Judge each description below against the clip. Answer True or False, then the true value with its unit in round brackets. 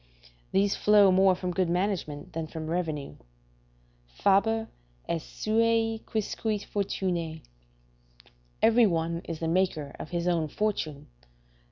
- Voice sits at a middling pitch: True (180 Hz)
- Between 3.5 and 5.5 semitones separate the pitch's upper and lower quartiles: True (4.2 semitones)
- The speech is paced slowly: True (120 wpm)